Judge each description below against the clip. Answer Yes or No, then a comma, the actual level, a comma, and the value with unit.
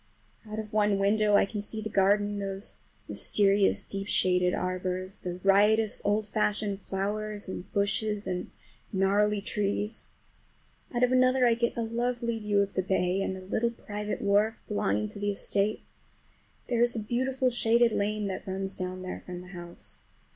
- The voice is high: Yes, high, 205 Hz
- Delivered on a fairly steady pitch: Yes, narrow, 2.1 semitones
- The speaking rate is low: No, average, 170 wpm